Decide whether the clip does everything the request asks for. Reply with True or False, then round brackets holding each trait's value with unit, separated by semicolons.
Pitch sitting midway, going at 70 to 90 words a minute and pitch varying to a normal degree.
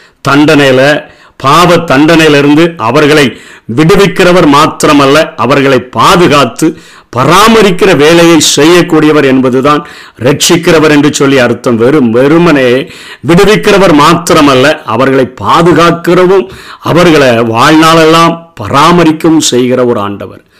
True (155 Hz; 80 wpm; 4.0 semitones)